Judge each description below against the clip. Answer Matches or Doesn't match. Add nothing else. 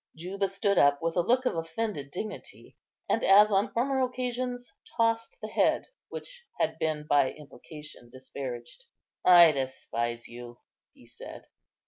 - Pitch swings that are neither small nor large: Doesn't match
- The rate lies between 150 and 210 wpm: Doesn't match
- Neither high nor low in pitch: Matches